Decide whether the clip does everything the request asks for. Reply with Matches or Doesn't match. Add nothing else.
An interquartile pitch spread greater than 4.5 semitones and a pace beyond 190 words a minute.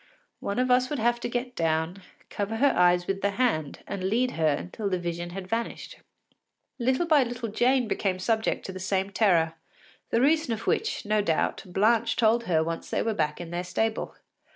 Matches